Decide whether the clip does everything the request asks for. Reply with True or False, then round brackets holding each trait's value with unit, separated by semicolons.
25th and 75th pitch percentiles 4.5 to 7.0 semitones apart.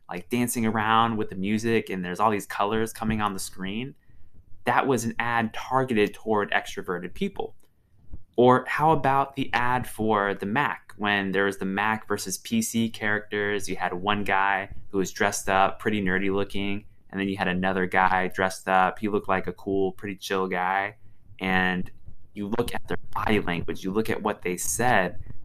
False (2.8 semitones)